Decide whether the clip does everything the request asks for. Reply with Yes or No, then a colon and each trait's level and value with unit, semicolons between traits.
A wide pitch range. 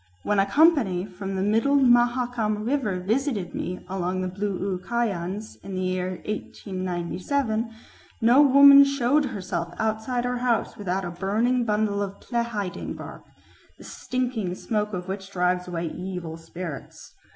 No: average, 4.7 semitones